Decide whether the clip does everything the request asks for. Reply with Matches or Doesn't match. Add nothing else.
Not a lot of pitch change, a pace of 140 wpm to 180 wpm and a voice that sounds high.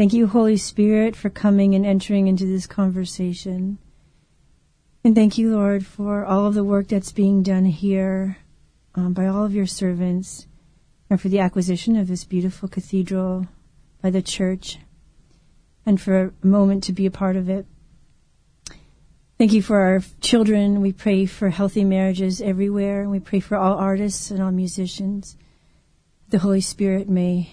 Matches